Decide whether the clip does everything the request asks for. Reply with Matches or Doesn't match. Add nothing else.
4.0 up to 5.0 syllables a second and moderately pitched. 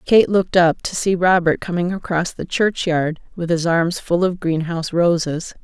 Matches